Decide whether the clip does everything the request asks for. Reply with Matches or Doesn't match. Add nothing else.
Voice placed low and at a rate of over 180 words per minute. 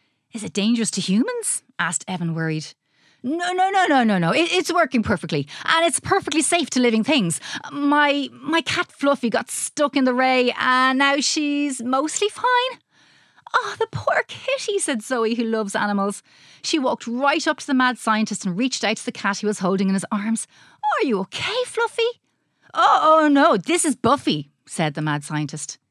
Doesn't match